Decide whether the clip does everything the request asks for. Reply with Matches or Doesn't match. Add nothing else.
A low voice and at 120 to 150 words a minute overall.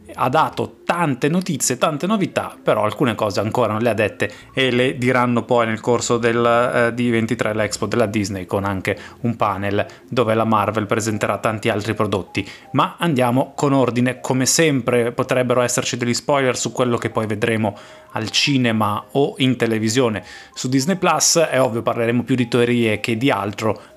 Doesn't match